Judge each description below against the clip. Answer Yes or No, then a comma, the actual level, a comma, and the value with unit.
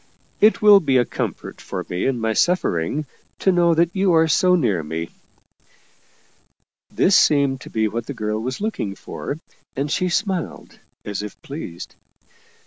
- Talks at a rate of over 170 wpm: No, average, 165 wpm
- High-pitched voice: No, medium, 140 Hz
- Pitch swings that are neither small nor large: No, wide, 8.5 semitones